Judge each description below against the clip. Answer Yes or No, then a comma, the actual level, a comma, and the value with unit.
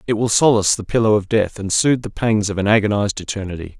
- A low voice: Yes, low, 105 Hz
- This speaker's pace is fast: Yes, fast, 235 wpm